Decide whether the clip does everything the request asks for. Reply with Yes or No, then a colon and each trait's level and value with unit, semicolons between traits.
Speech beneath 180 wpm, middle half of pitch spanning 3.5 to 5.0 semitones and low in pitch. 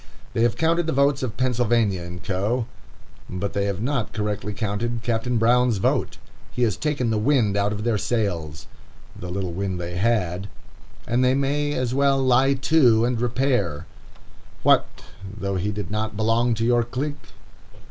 Yes: average, 170 wpm; average, 4.0 semitones; low, 115 Hz